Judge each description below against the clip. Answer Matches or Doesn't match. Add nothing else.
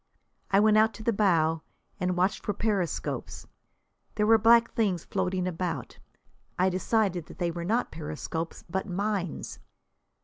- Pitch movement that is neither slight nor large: Matches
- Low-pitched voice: Doesn't match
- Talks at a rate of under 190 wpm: Matches